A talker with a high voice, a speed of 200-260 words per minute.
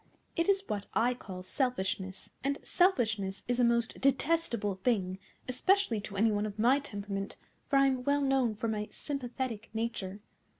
No: high, 235 Hz; average, 165 wpm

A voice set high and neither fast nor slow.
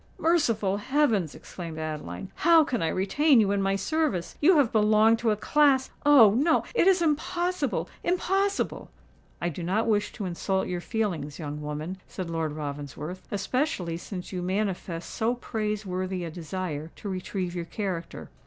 Yes: high, 195 Hz; average, 150 wpm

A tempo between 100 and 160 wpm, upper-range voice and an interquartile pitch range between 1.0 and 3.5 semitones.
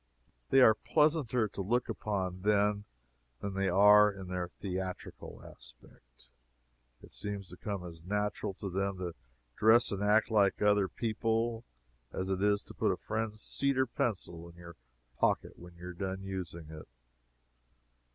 No: average, 155 wpm; low, 100 Hz; average, 2.9 semitones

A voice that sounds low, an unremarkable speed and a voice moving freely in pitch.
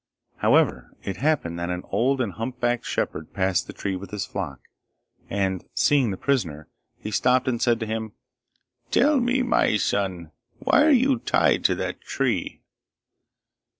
Yes: low, 110 Hz; average, 155 wpm; wide, 6.3 semitones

